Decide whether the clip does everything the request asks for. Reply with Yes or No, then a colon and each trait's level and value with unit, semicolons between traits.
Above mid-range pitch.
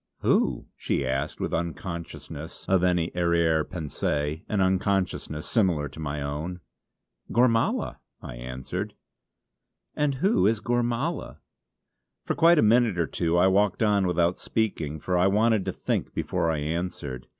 No: very low, 90 Hz